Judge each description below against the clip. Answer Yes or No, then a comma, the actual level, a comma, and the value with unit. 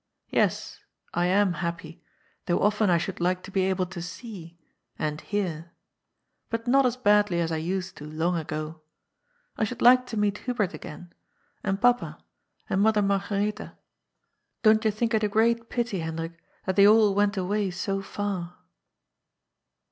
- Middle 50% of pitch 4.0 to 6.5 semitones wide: No, average, 3.6 semitones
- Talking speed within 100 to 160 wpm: No, average, 170 wpm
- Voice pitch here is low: No, high, 195 Hz